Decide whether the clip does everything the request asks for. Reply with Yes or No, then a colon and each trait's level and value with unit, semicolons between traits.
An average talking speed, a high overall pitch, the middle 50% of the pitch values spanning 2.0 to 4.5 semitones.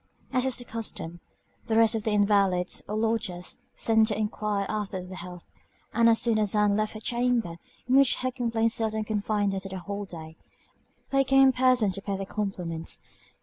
Yes: average, 190 wpm; high, 215 Hz; average, 2.8 semitones